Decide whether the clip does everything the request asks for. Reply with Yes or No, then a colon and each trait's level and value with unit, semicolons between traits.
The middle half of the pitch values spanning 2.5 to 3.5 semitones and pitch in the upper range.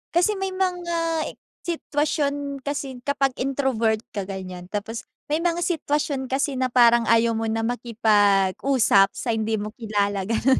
No: average, 4.8 semitones; very high, 255 Hz